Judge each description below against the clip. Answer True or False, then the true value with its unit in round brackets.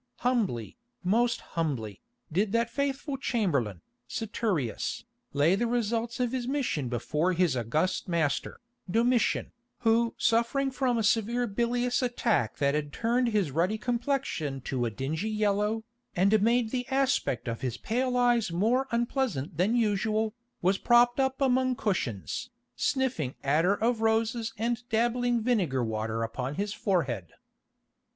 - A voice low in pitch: False (220 Hz)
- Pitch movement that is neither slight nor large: False (7.6 semitones)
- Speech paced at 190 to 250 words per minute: False (135 wpm)